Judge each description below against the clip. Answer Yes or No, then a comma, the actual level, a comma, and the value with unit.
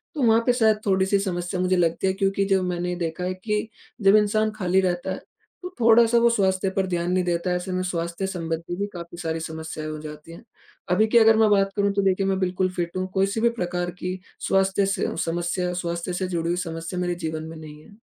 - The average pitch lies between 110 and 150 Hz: No, medium, 185 Hz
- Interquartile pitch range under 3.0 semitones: Yes, narrow, 2.5 semitones